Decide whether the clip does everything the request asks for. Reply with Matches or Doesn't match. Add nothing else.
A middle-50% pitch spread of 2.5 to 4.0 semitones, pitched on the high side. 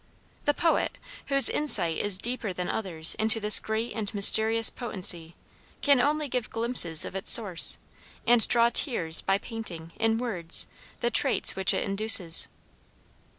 Doesn't match